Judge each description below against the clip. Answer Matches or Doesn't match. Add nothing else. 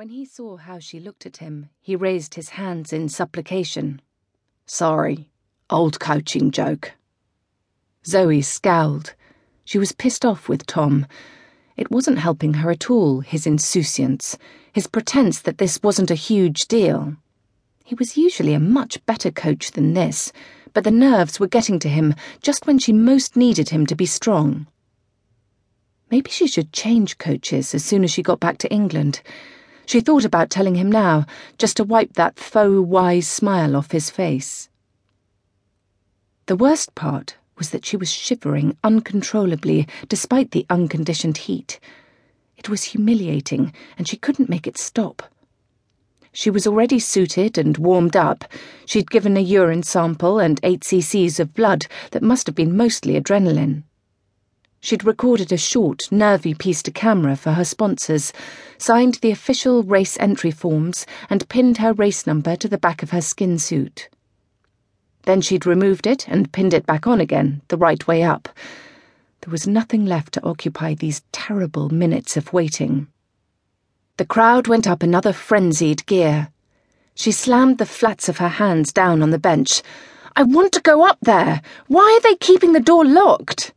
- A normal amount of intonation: Doesn't match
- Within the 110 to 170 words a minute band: Matches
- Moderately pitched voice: Matches